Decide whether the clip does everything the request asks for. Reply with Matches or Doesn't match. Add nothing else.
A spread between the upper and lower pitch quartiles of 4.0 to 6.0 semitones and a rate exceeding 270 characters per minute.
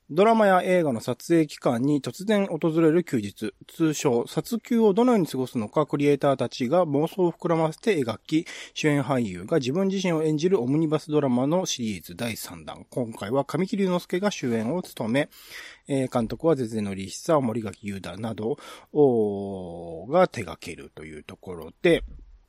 Doesn't match